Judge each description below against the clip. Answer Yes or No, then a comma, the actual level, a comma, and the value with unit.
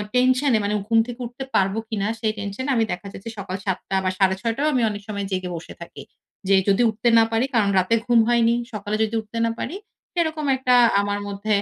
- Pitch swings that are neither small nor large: Yes, average, 3.2 semitones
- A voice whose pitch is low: No, high, 220 Hz